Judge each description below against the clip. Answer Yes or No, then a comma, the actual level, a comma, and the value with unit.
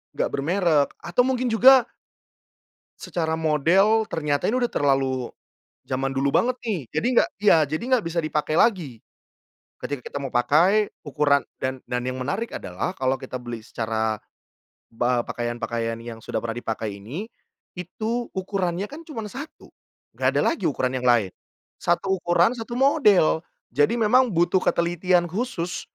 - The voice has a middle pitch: Yes, medium, 160 Hz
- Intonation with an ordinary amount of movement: No, wide, 8.4 semitones